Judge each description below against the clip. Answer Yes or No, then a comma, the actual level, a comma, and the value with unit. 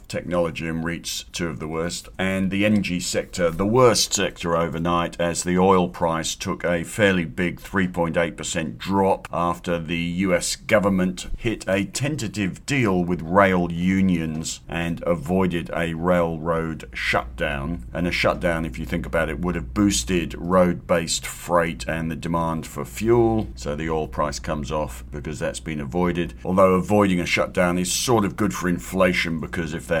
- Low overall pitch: Yes, very low, 85 Hz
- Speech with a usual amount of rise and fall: No, narrow, 2.3 semitones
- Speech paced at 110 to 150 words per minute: No, average, 165 wpm